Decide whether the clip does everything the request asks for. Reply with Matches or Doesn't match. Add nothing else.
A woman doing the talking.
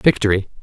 Doesn't match